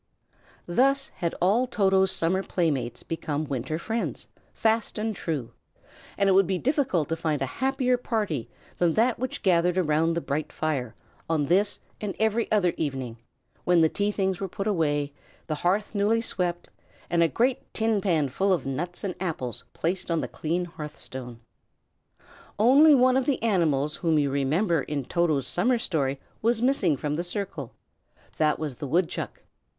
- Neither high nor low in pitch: Yes, medium, 175 Hz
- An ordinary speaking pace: Yes, average, 170 wpm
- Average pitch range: No, wide, 5.8 semitones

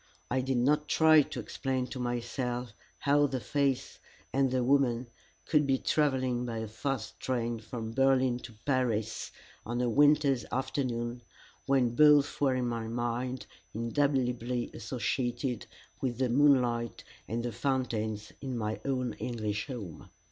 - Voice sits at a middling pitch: No, low, 125 Hz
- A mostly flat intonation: Yes, narrow, 2.3 semitones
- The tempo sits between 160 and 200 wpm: No, average, 140 wpm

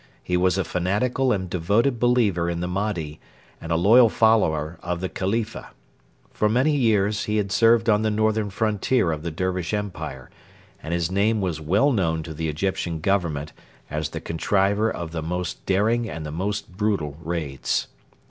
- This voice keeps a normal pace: Yes, average, 175 wpm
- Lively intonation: No, average, 4.7 semitones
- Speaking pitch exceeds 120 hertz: No, very low, 95 Hz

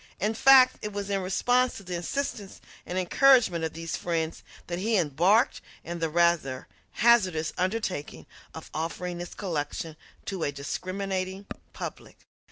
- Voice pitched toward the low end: No, medium, 185 Hz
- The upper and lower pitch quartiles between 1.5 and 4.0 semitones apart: Yes, average, 3.7 semitones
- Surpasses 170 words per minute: No, average, 145 wpm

